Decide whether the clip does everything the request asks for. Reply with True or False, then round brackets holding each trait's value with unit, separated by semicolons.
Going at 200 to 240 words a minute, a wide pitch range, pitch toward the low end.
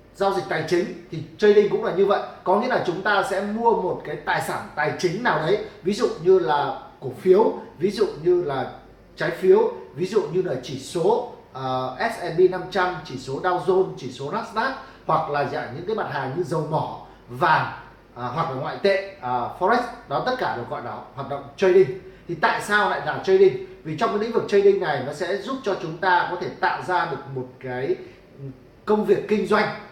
False (220 wpm; 6.3 semitones; 185 Hz)